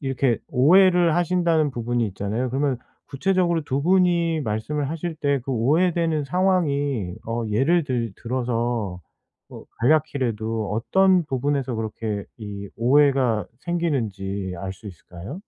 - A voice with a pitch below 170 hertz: Yes, low, 135 Hz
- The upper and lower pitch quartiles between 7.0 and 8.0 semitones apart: No, wide, 6.4 semitones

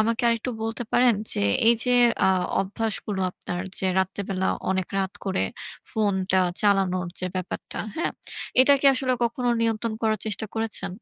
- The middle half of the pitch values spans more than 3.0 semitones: Yes, average, 3.4 semitones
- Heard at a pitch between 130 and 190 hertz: No, high, 215 Hz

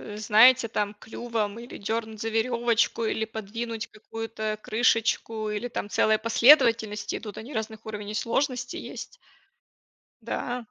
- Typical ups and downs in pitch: No, narrow, 1.5 semitones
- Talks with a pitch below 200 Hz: No, high, 225 Hz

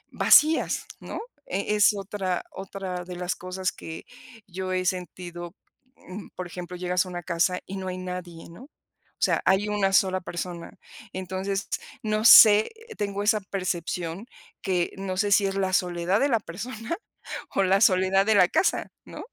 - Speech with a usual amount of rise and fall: No, narrow, 1.8 semitones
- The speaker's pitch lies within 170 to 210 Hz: Yes, medium, 185 Hz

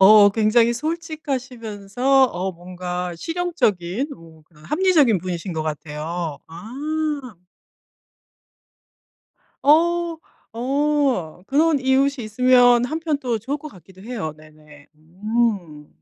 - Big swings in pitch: Yes, wide, 7.9 semitones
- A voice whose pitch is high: Yes, high, 220 Hz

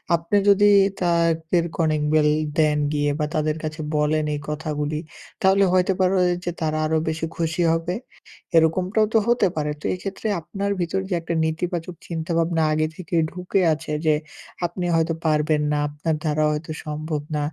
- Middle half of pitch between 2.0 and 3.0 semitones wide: Yes, narrow, 2.5 semitones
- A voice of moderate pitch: Yes, medium, 160 Hz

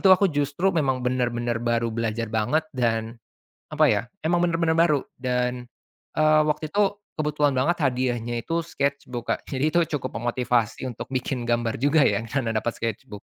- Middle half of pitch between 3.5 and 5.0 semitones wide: Yes, average, 4.4 semitones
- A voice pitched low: Yes, low, 130 Hz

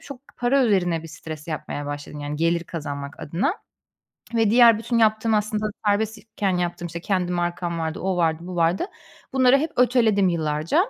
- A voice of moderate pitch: Yes, medium, 180 Hz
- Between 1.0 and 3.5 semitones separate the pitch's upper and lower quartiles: No, average, 5.2 semitones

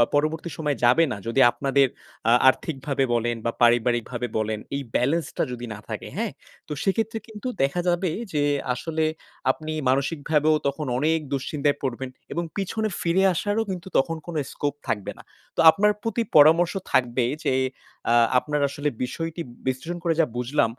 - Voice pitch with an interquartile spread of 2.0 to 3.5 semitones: No, average, 4.6 semitones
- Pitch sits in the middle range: Yes, medium, 150 Hz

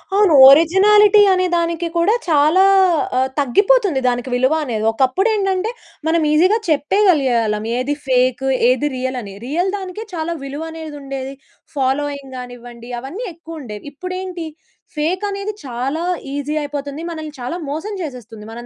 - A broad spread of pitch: Yes, wide, 5.9 semitones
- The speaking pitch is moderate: No, very high, 295 Hz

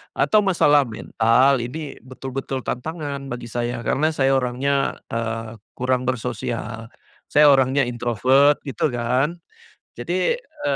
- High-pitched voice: No, low, 130 Hz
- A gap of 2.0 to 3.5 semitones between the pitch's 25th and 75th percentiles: Yes, average, 3.2 semitones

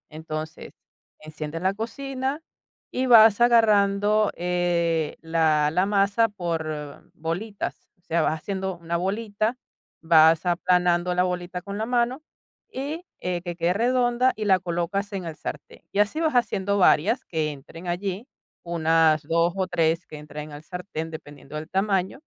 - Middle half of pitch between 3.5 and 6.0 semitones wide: Yes, average, 4.2 semitones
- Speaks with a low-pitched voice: No, medium, 180 Hz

